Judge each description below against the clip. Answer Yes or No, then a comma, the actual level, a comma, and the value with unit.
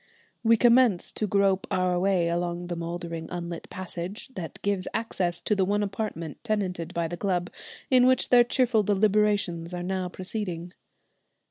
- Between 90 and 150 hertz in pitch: No, medium, 185 Hz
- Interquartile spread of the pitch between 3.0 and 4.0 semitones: Yes, average, 3.3 semitones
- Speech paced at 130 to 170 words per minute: Yes, average, 155 wpm